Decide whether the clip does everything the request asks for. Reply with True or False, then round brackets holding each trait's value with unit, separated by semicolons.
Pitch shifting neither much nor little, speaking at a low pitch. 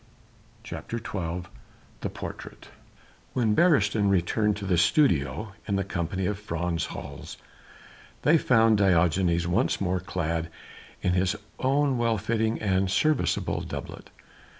True (4.2 semitones; 100 Hz)